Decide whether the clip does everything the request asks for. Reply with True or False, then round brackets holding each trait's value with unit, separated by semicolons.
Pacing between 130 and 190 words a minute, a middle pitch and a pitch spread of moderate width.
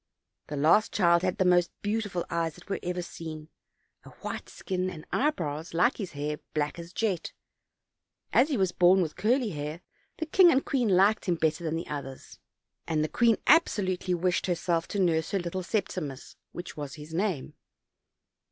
True (180 wpm; 175 Hz; 3.8 semitones)